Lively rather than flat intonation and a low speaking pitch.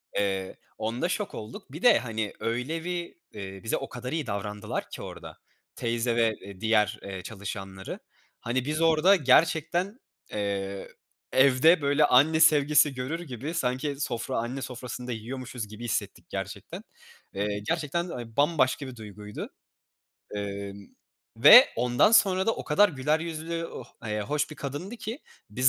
Yes: wide, 6.6 semitones; low, 130 Hz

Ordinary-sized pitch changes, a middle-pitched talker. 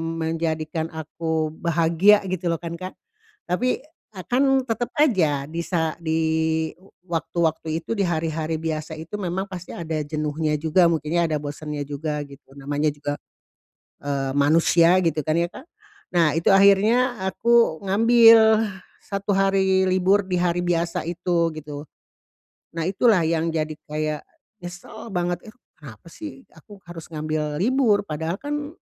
Yes: average, 3.7 semitones; medium, 170 Hz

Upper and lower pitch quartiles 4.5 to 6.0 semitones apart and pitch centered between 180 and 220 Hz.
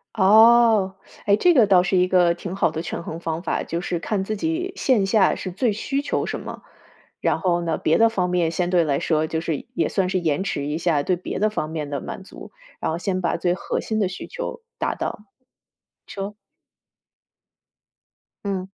No: average, 3.8 semitones; medium, 185 Hz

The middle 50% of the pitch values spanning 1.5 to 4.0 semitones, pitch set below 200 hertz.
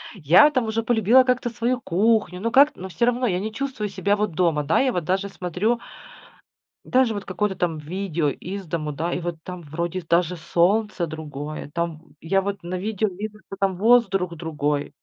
No: average, 4.5 semitones; medium, 185 Hz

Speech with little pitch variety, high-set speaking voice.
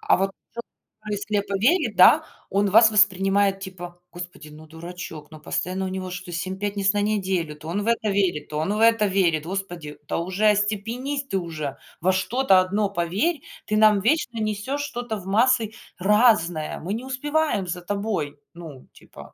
No: average, 3.5 semitones; high, 195 Hz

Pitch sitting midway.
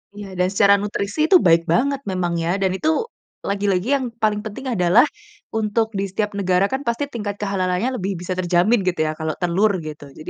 No: high, 200 Hz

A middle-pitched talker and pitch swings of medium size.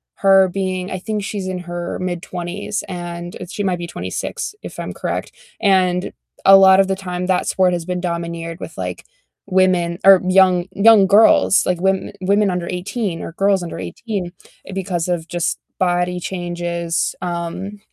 No: medium, 180 Hz; narrow, 1.8 semitones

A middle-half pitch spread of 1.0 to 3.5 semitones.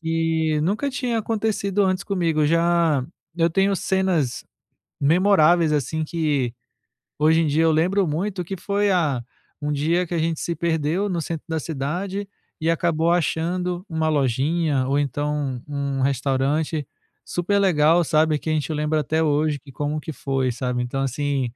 Yes: average, 3.2 semitones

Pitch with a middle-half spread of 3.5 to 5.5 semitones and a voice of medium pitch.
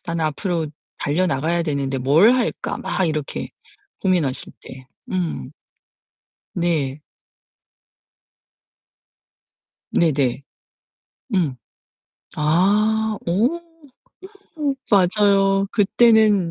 Yes: average, 5.2 semitones; medium, 175 Hz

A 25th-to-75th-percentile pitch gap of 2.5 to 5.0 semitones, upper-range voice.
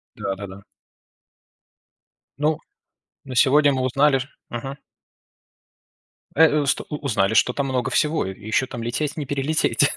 No: average, 3.6 semitones; low, 135 Hz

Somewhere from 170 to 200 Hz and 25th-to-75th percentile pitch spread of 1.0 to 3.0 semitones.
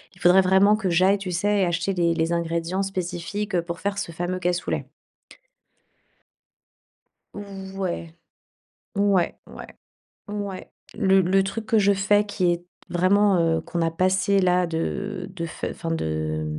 Yes: medium, 185 Hz; narrow, 2.6 semitones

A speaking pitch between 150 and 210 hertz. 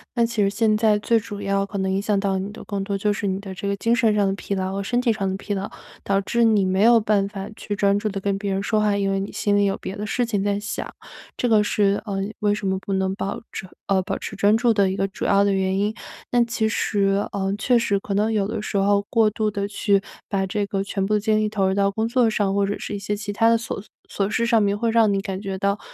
Yes: high, 200 Hz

